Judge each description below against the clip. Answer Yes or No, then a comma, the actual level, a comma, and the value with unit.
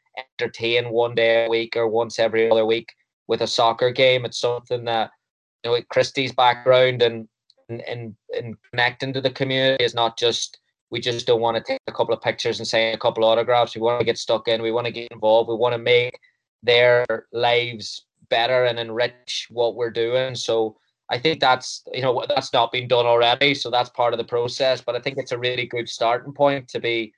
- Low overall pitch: Yes, low, 120 Hz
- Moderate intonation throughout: No, narrow, 1.6 semitones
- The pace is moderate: No, fast, 220 wpm